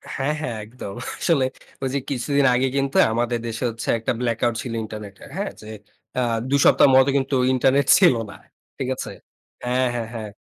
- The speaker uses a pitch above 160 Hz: No, low, 125 Hz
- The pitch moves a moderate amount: Yes, average, 3.0 semitones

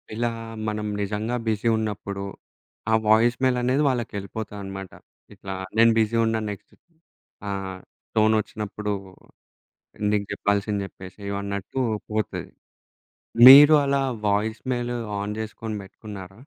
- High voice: No, low, 105 Hz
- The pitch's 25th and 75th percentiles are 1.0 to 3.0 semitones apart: Yes, narrow, 2.4 semitones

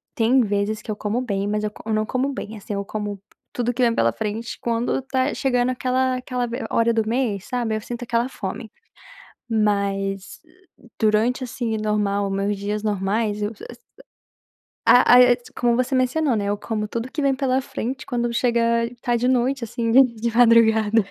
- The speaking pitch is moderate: No, high, 230 Hz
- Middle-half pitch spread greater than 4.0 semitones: No, average, 2.9 semitones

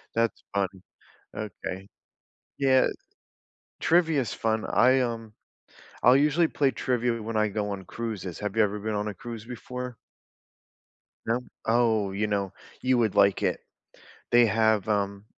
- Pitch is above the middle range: No, low, 110 Hz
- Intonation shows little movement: No, average, 3.1 semitones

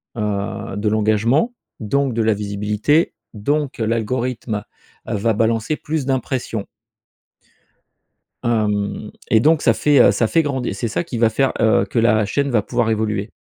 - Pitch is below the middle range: Yes, low, 115 Hz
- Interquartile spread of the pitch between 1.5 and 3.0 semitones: No, average, 3.8 semitones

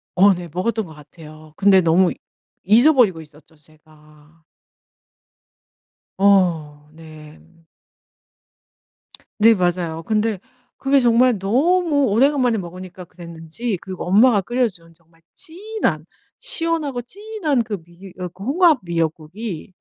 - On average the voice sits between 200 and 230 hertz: No, high, 190 Hz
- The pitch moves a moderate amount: No, wide, 6.9 semitones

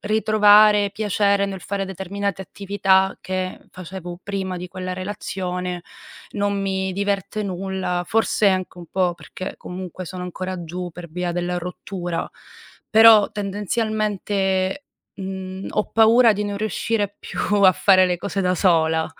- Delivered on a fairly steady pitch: Yes, narrow, 2.0 semitones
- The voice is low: No, high, 190 Hz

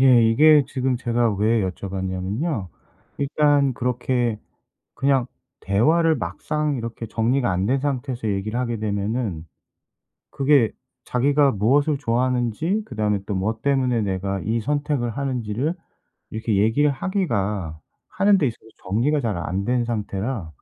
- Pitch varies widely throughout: No, average, 5.0 semitones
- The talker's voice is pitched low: Yes, low, 120 Hz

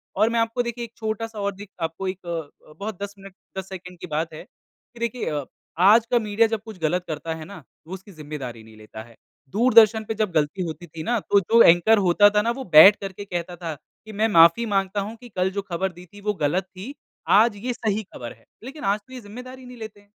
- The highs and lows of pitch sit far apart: No, average, 4.6 semitones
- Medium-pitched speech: No, high, 200 Hz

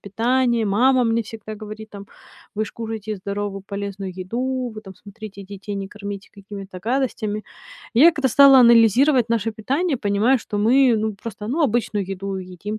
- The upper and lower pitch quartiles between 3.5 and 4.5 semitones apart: No, average, 3.1 semitones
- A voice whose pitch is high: Yes, high, 215 Hz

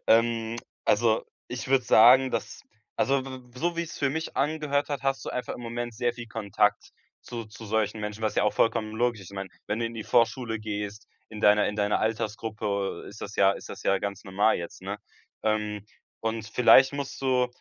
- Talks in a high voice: No, low, 115 Hz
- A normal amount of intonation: Yes, average, 3.0 semitones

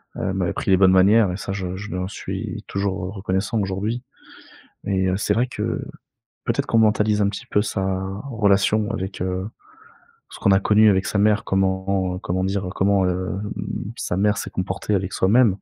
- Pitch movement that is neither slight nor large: No, narrow, 1.8 semitones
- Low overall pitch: Yes, low, 100 Hz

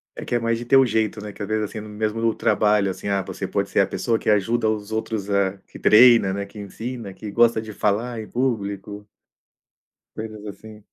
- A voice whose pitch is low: Yes, low, 105 Hz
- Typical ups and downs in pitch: No, narrow, 2.2 semitones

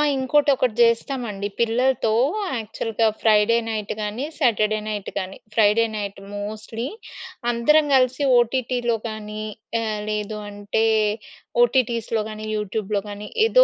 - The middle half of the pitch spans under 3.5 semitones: Yes, narrow, 2.5 semitones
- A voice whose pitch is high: Yes, high, 225 Hz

